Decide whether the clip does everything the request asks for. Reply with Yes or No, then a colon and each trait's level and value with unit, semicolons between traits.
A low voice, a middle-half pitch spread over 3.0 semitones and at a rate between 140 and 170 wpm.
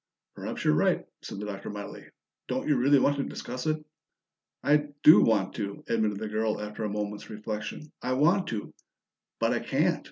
No: low, 110 Hz; average, 5.2 semitones; average, 185 wpm